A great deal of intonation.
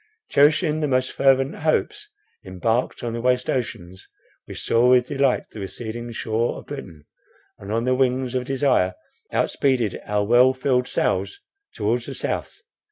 No: average, 2.9 semitones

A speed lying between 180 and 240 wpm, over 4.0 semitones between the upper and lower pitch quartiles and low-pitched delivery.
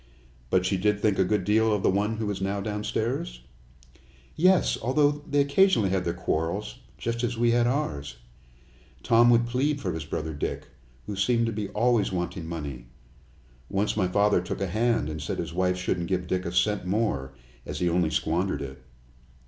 Yes: average, 190 wpm; average, 4.8 semitones; low, 100 Hz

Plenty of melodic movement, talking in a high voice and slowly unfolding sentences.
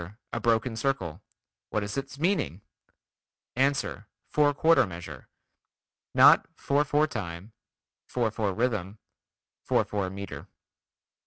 No: wide, 6.2 semitones; low, 110 Hz; slow, 110 wpm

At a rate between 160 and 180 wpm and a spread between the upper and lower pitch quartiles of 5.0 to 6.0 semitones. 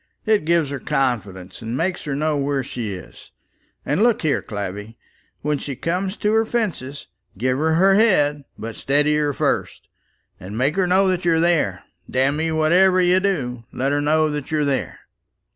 Yes: average, 175 wpm; wide, 5.5 semitones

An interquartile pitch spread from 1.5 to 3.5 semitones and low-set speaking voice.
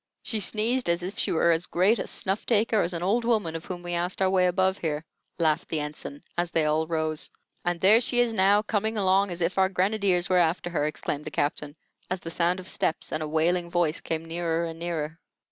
No: average, 2.9 semitones; medium, 175 Hz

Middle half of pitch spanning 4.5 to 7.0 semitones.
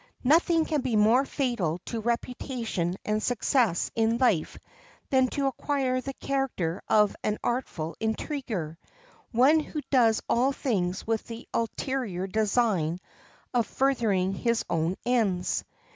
Yes: average, 5.1 semitones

